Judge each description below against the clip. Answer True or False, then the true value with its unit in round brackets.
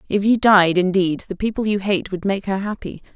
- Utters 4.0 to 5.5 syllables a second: True (5.3 syllables/s)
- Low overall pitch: False (195 Hz)